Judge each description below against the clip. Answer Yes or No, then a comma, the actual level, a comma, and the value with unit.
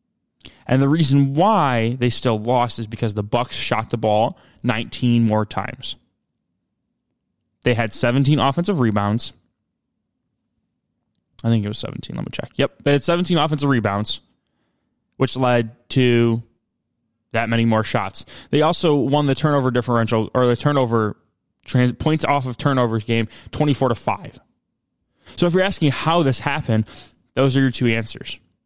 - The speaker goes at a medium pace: Yes, average, 150 wpm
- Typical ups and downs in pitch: Yes, average, 3.8 semitones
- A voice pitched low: Yes, low, 125 Hz